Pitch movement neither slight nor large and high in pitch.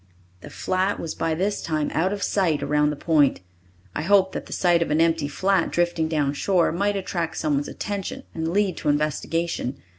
No: average, 3.8 semitones; medium, 165 Hz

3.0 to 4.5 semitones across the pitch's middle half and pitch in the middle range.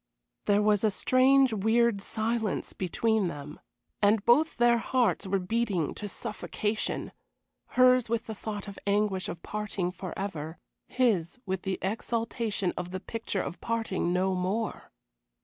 No: average, 3.5 semitones; high, 210 Hz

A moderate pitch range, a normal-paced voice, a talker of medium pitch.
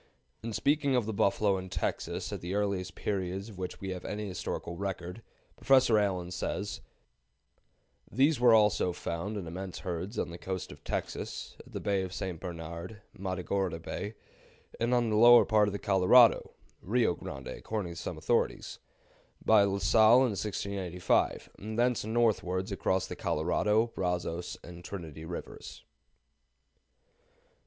No: average, 3.4 semitones; average, 150 wpm; very low, 95 Hz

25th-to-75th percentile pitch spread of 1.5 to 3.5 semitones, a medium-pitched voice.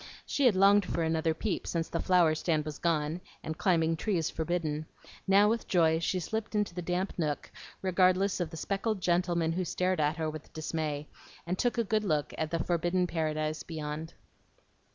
Yes: average, 2.8 semitones; medium, 170 Hz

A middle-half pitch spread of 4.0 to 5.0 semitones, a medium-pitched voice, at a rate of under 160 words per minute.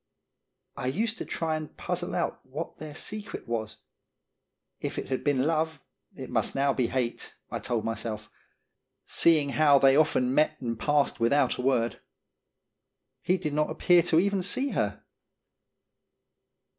Yes: average, 4.3 semitones; medium, 145 Hz; average, 150 wpm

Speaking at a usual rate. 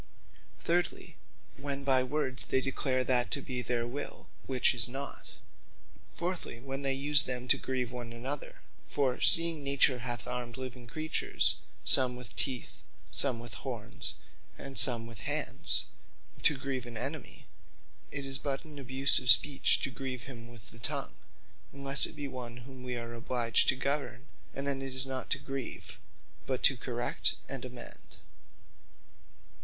Yes: average, 160 wpm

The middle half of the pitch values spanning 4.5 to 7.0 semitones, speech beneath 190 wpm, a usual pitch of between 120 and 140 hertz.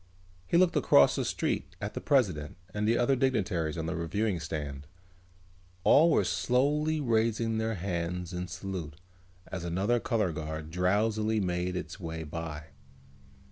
No: wide, 5.5 semitones; average, 145 wpm; very low, 90 Hz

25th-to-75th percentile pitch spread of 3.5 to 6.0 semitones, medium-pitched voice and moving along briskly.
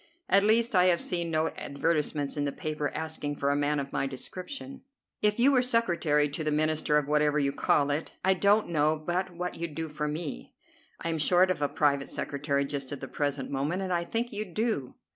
Yes: average, 4.0 semitones; medium, 155 Hz; fast, 220 wpm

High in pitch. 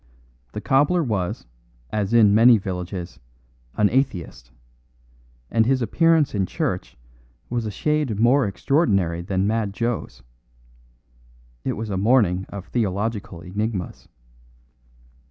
No: low, 105 Hz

